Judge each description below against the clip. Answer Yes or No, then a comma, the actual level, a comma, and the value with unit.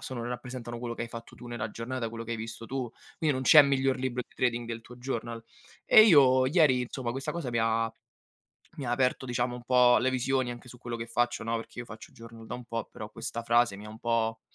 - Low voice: Yes, low, 120 Hz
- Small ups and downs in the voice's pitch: Yes, narrow, 1.9 semitones